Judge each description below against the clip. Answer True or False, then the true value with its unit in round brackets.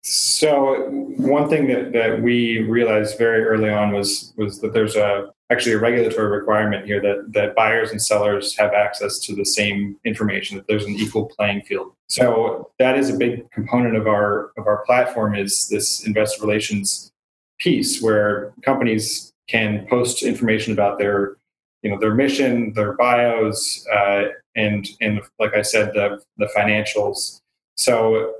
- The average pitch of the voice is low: True (105 Hz)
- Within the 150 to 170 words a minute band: True (160 wpm)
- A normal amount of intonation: False (2.1 semitones)